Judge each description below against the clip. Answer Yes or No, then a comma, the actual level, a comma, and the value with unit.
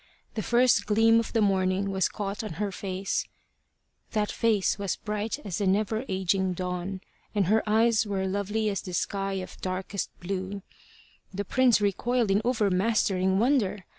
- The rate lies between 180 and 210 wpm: No, average, 160 wpm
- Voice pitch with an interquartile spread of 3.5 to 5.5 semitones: No, narrow, 2.4 semitones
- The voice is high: Yes, high, 200 Hz